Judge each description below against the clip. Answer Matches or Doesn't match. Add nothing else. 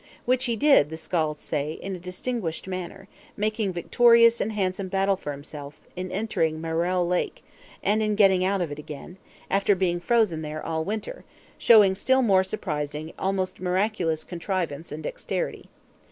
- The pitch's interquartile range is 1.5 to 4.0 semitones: Doesn't match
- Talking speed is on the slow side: Doesn't match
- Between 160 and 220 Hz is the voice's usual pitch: Matches